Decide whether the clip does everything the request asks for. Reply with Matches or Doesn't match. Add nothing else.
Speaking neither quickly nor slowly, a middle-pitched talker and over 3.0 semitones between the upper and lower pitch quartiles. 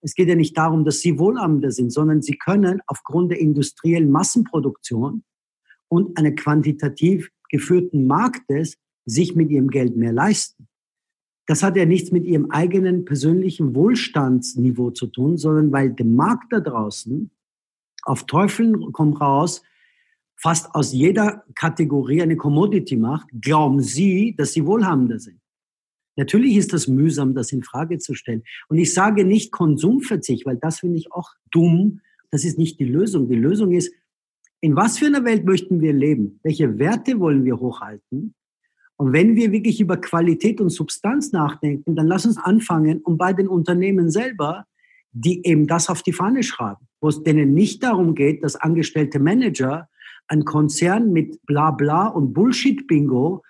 Matches